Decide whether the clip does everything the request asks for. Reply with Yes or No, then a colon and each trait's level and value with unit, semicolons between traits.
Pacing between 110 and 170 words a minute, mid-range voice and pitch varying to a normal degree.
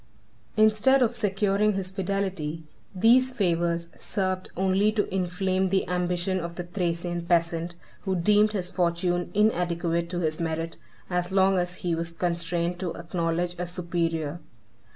No: average, 145 wpm; medium, 180 Hz; narrow, 2.3 semitones